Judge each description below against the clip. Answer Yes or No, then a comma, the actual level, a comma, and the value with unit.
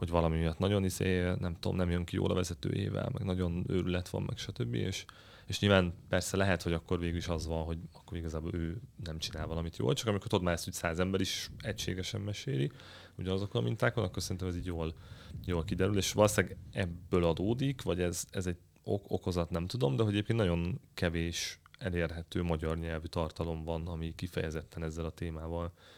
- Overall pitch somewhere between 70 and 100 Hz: Yes, very low, 90 Hz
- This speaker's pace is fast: Yes, fast, 195 wpm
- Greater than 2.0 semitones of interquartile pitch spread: Yes, average, 2.7 semitones